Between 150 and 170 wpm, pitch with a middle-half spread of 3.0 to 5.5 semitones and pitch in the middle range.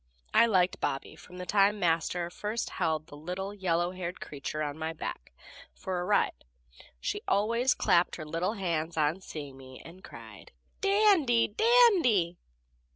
Yes: average, 160 wpm; average, 4.6 semitones; medium, 180 Hz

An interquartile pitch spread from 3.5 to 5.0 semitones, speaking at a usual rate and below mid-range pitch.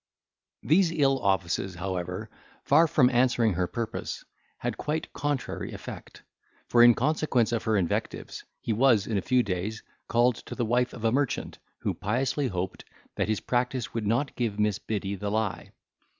Yes: average, 3.9 semitones; average, 170 wpm; low, 115 Hz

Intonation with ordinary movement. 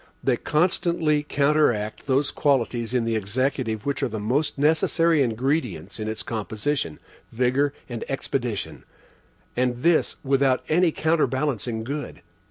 Yes: average, 4.6 semitones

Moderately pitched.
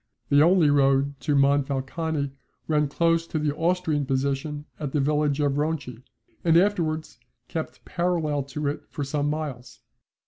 Yes: medium, 150 Hz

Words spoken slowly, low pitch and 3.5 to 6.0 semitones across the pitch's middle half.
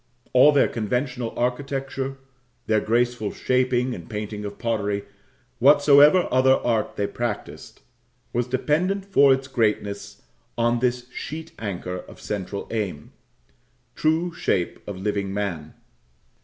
Yes: slow, 120 wpm; low, 120 Hz; average, 4.7 semitones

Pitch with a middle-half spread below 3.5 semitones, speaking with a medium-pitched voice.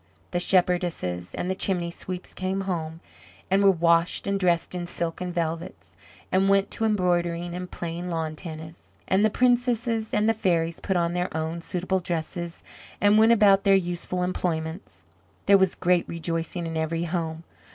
Yes: narrow, 2.5 semitones; medium, 175 Hz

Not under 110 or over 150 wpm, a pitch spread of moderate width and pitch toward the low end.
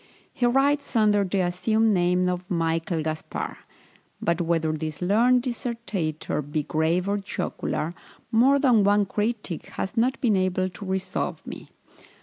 No: average, 140 wpm; average, 5.0 semitones; high, 190 Hz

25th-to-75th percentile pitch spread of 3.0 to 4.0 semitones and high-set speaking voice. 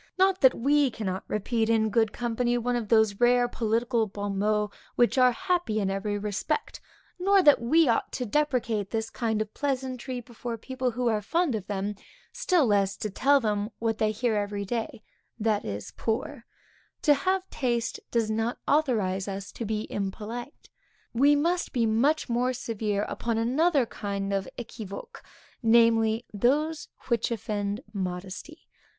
Yes: average, 3.6 semitones; high, 230 Hz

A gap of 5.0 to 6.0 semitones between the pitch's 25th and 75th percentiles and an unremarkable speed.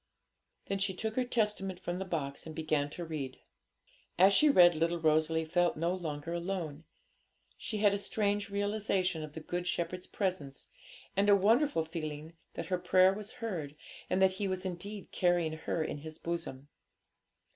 No: average, 3.7 semitones; average, 170 wpm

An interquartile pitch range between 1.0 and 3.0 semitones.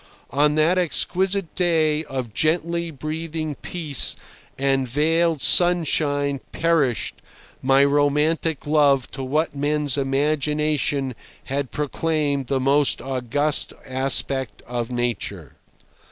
Yes: average, 2.7 semitones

